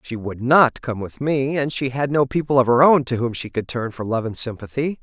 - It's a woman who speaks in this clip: No, male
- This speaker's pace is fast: Yes, fast, 275 wpm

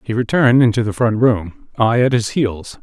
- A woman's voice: No, male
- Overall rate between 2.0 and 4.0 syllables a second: No, 5.0 syllables/s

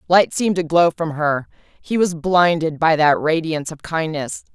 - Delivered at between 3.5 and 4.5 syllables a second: No, 4.9 syllables/s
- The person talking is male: No, female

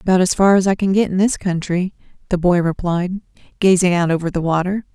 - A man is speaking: No, female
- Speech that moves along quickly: Yes, fast, 220 wpm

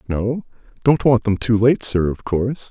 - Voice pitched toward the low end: Yes, low, 115 Hz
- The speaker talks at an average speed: Yes, average, 180 wpm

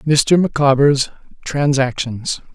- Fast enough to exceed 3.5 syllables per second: No, 3.3 syllables/s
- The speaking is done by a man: Yes, male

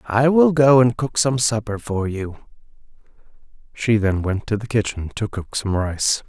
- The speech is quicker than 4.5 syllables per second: No, 4.4 syllables/s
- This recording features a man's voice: Yes, male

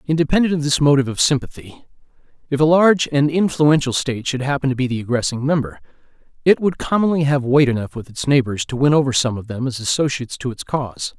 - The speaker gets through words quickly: Yes, fast, 210 wpm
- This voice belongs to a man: Yes, male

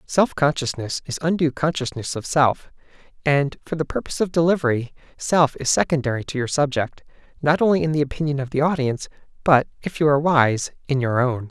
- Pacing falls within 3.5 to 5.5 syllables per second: No, 5.9 syllables/s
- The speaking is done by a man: Yes, male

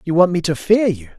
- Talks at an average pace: No, fast, 305 wpm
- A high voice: No, medium, 170 Hz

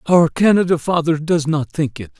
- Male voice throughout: Yes, male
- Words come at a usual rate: Yes, average, 190 wpm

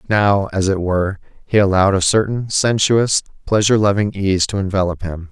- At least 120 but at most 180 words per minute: Yes, average, 170 wpm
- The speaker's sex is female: No, male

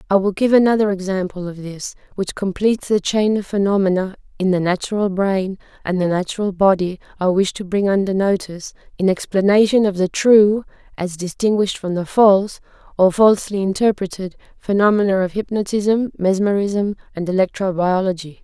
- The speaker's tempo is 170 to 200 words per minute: No, average, 155 wpm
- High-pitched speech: Yes, high, 195 Hz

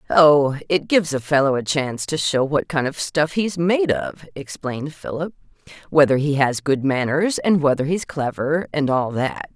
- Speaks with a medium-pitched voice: Yes, medium, 150 Hz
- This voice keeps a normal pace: Yes, average, 180 wpm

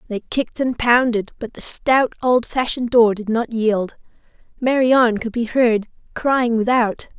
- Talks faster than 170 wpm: No, average, 150 wpm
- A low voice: No, high, 235 Hz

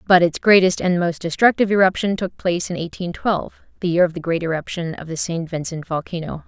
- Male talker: No, female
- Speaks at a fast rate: Yes, fast, 215 wpm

